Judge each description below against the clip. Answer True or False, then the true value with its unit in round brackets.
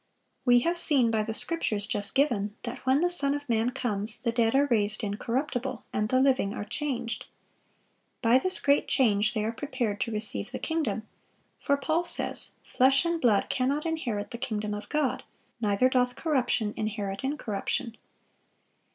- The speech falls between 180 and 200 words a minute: False (170 wpm)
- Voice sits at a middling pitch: False (245 Hz)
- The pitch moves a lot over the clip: False (4.6 semitones)